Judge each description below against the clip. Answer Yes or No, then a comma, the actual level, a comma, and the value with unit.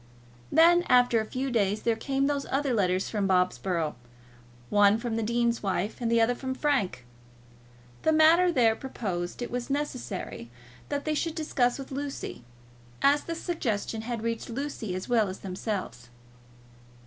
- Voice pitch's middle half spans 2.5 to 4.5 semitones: No, wide, 5.4 semitones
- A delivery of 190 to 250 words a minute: No, average, 160 wpm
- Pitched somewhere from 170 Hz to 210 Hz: No, high, 235 Hz